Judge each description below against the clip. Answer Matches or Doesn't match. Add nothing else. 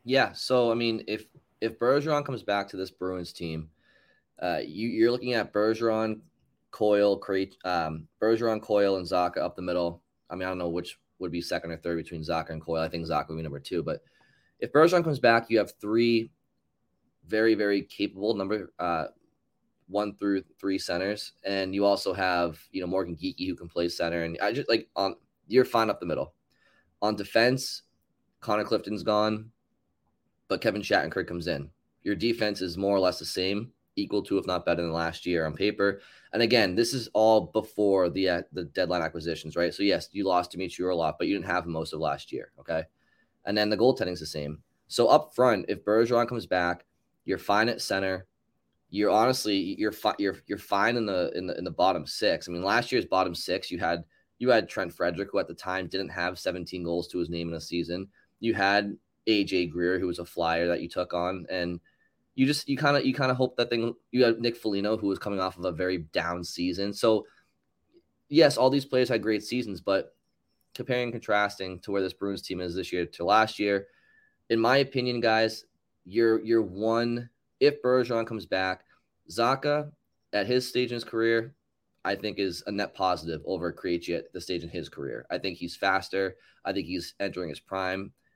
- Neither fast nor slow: Doesn't match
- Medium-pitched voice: Doesn't match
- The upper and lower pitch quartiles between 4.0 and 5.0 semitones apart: Matches